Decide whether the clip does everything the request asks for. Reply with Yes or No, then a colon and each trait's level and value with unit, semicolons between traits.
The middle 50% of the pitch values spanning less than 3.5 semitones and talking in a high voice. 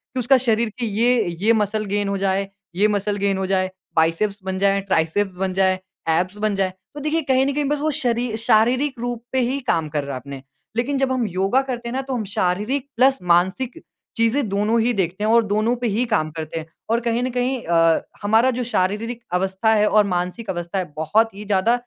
No: average, 4.3 semitones; high, 210 Hz